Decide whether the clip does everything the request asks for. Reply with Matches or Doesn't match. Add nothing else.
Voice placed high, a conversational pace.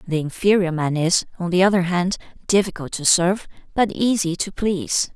Doesn't match